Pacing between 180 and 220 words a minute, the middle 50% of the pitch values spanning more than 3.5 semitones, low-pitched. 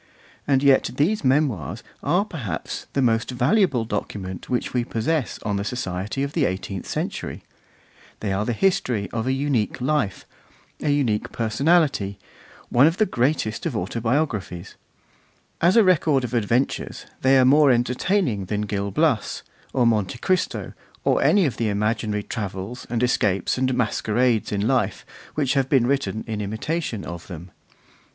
No: average, 155 wpm; average, 5.0 semitones; low, 120 Hz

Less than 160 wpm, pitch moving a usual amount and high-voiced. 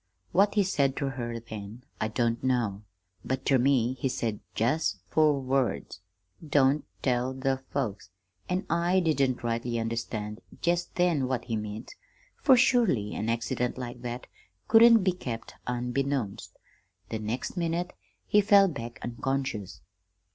No: average, 140 wpm; average, 4.9 semitones; low, 130 Hz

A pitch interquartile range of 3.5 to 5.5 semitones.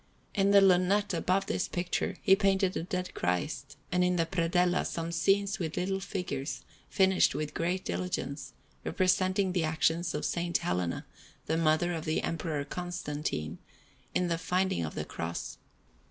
No: average, 3.0 semitones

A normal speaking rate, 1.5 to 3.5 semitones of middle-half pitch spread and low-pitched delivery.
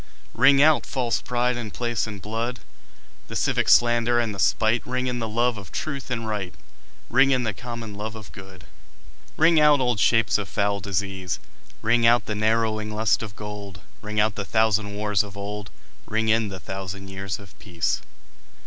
Yes: average, 185 wpm; average, 2.9 semitones; low, 110 Hz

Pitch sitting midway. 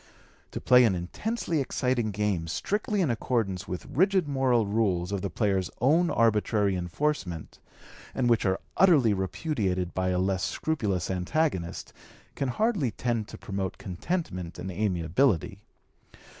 No: low, 105 Hz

